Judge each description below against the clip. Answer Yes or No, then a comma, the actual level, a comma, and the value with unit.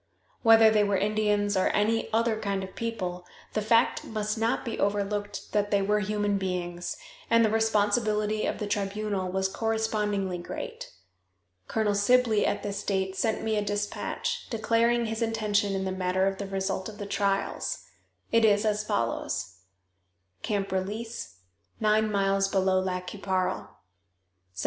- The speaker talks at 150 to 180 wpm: Yes, average, 155 wpm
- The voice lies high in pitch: Yes, high, 205 Hz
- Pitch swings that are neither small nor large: No, narrow, 2.2 semitones